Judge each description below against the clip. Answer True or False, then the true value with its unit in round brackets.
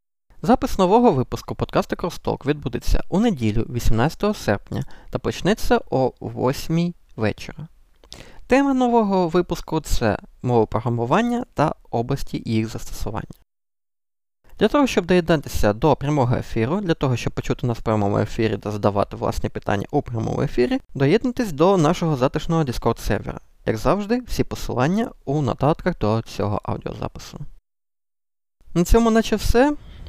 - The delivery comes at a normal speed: True (130 wpm)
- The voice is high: False (130 Hz)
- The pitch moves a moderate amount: False (8.2 semitones)